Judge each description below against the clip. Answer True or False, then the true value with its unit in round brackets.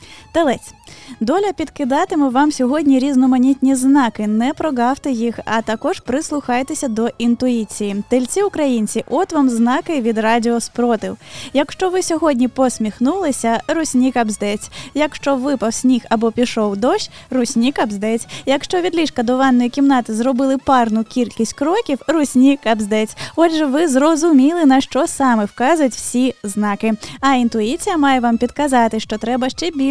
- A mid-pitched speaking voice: False (260 Hz)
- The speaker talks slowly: False (135 wpm)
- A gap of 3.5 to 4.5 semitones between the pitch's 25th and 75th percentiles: True (3.8 semitones)